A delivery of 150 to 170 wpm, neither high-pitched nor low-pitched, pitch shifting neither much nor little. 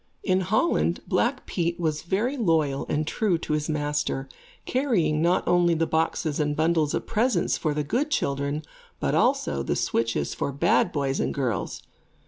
Yes: average, 165 wpm; medium, 160 Hz; average, 3.7 semitones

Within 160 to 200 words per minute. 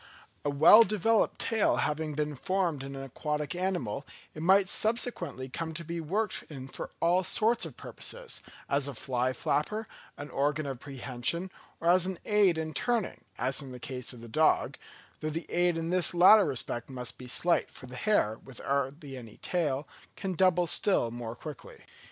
Yes: average, 180 wpm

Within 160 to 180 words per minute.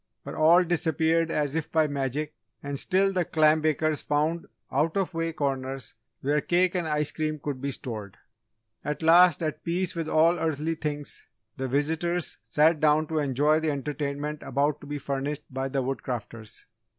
Yes: average, 170 wpm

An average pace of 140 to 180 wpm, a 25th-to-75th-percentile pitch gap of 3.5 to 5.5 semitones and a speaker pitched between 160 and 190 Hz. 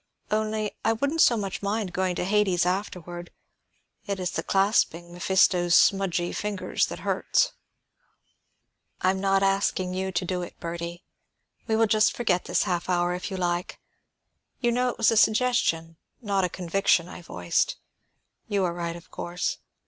No: average, 165 wpm; average, 3.1 semitones; medium, 185 Hz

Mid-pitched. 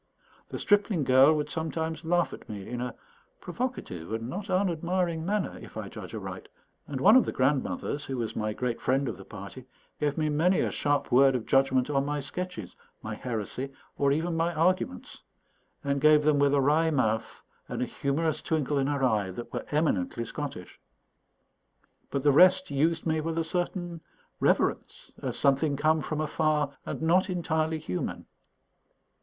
Yes: medium, 150 Hz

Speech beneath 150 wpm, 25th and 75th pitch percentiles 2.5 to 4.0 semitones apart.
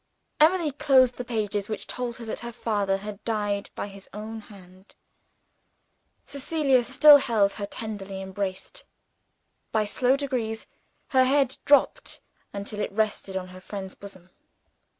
No: average, 140 wpm; average, 4.4 semitones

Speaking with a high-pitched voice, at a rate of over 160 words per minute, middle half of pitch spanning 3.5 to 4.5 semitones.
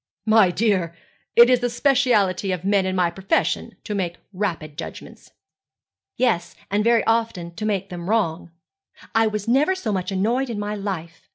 Yes: high, 205 Hz; average, 170 wpm; average, 3.9 semitones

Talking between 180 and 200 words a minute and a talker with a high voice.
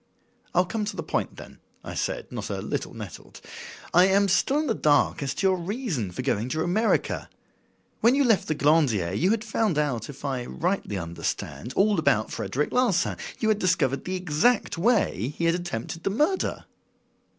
No: average, 185 wpm; medium, 175 Hz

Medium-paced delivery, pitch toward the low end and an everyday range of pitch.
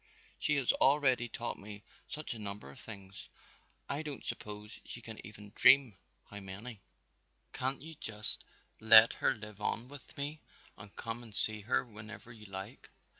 Yes: average, 165 wpm; low, 110 Hz; average, 3.6 semitones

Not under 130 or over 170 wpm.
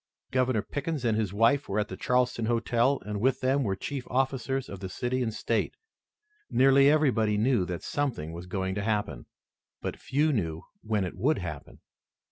No: average, 180 wpm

